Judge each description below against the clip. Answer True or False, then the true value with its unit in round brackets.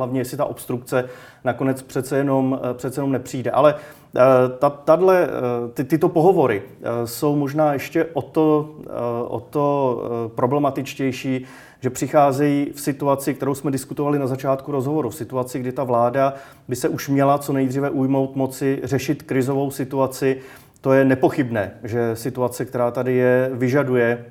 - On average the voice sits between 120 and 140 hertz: True (135 Hz)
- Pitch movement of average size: False (2.2 semitones)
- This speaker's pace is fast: False (145 wpm)